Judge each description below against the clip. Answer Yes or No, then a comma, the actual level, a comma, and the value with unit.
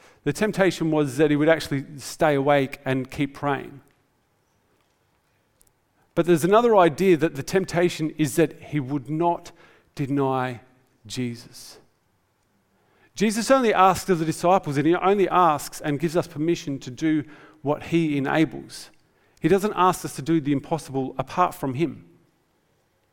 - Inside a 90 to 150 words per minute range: Yes, average, 145 wpm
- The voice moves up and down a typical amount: Yes, average, 4.0 semitones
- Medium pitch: Yes, medium, 150 Hz